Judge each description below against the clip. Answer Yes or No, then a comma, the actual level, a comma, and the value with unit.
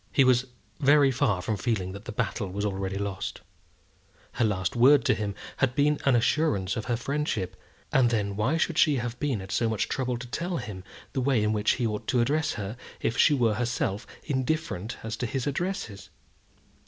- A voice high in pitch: No, low, 120 Hz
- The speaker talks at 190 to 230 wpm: Yes, average, 200 wpm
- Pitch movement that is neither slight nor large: Yes, average, 4.7 semitones